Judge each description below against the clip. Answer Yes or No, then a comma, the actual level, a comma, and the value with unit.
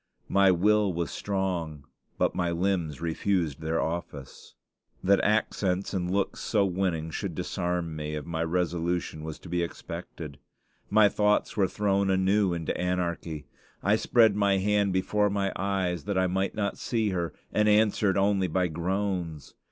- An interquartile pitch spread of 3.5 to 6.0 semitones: No, average, 2.9 semitones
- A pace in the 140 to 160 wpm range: Yes, average, 155 wpm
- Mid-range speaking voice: No, very low, 95 Hz